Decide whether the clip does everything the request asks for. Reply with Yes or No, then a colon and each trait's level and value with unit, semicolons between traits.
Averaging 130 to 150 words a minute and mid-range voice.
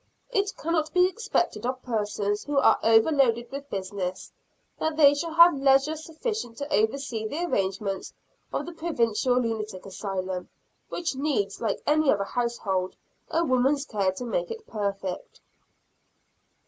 No: average, 145 wpm; very high, 250 Hz